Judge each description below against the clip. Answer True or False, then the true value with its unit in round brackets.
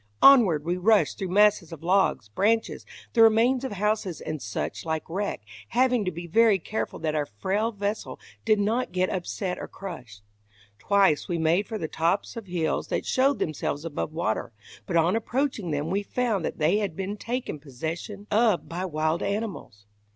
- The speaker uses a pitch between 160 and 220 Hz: True (190 Hz)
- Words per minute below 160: False (180 wpm)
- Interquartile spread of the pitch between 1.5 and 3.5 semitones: False (5.1 semitones)